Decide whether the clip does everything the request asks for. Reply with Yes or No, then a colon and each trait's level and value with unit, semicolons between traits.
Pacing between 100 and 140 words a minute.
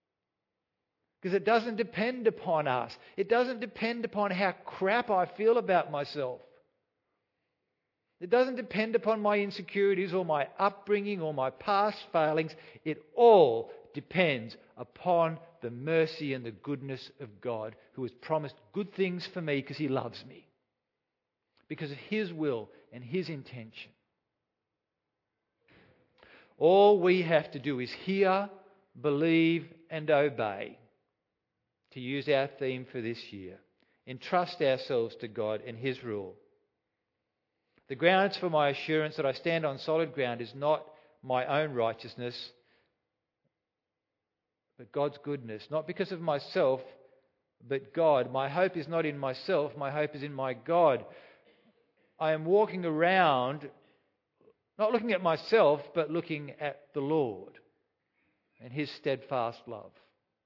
Yes: slow, 135 wpm